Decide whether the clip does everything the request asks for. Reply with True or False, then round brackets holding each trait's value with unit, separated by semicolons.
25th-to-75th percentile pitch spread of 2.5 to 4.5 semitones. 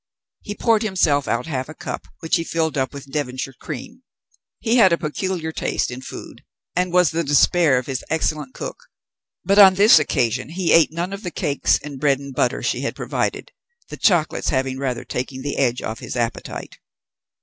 False (5.1 semitones)